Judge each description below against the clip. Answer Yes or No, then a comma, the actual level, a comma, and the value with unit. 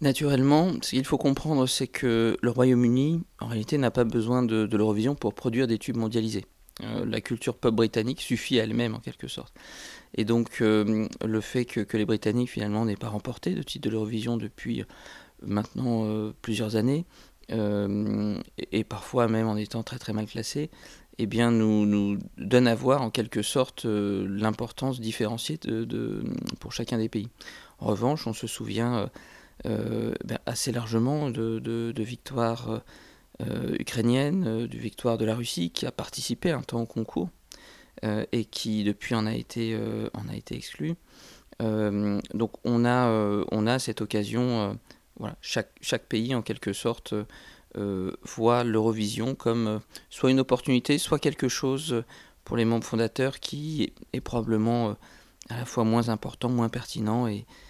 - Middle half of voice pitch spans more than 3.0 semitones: No, narrow, 2.4 semitones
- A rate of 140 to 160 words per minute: No, average, 175 wpm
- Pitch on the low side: Yes, low, 115 Hz